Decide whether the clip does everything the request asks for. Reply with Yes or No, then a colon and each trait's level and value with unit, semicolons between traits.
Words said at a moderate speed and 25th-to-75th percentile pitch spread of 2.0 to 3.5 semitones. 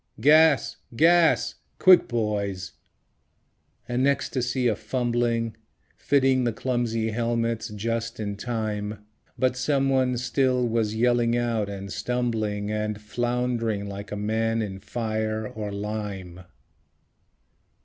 No: slow, 110 wpm; average, 2.7 semitones